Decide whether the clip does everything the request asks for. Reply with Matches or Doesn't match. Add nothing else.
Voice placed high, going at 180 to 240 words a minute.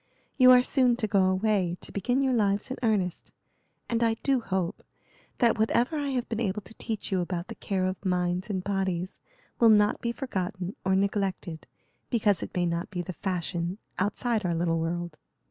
Matches